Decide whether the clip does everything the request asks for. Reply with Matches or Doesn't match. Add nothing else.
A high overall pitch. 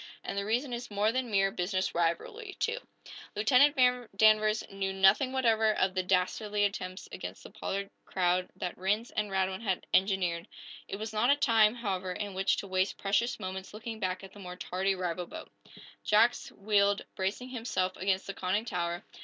Matches